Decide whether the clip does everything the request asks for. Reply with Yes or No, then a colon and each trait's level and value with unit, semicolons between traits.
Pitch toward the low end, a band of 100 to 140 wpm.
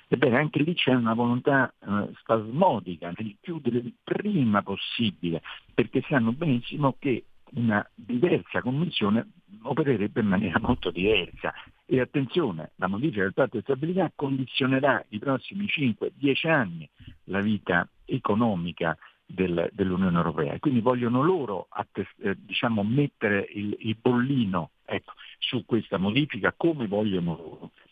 Yes: low, 125 Hz; average, 130 wpm